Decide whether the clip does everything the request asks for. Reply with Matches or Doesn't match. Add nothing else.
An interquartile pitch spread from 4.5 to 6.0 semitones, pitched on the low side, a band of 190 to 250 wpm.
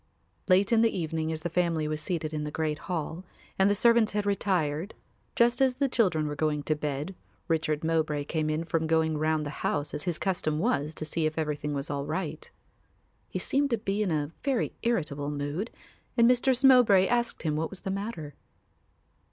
Doesn't match